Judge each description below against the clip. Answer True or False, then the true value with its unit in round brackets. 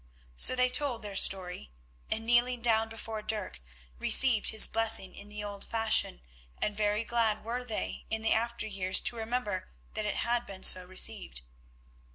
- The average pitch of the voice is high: True (220 Hz)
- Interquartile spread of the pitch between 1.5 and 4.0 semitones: True (2.4 semitones)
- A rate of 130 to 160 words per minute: False (170 wpm)